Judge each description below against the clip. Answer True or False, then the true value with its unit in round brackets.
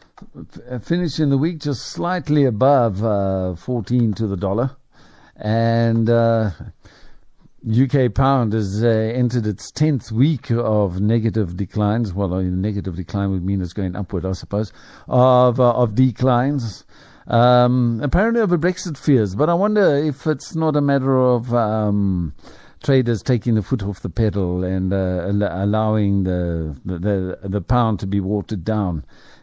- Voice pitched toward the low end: True (115 Hz)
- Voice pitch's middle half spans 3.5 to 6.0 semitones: True (4.5 semitones)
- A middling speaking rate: True (150 wpm)